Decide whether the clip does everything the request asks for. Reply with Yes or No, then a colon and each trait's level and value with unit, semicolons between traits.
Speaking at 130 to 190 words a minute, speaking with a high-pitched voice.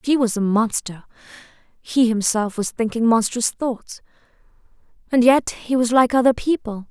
Yes: average, 140 wpm; high, 235 Hz